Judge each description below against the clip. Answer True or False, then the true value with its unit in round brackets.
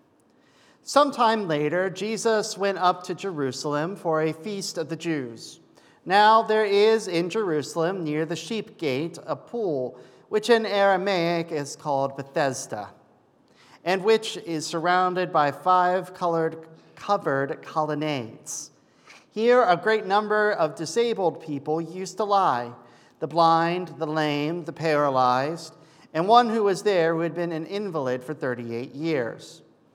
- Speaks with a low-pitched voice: False (170 Hz)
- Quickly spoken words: False (140 wpm)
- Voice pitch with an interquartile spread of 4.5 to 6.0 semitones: True (4.9 semitones)